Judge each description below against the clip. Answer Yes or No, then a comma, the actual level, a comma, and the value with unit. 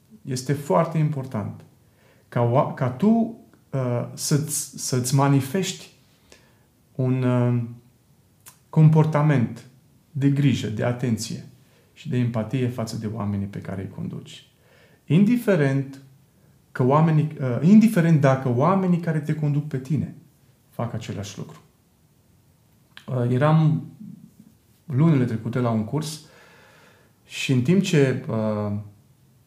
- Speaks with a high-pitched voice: No, low, 135 Hz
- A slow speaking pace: Yes, slow, 110 wpm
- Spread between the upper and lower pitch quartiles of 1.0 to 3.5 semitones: No, average, 4.2 semitones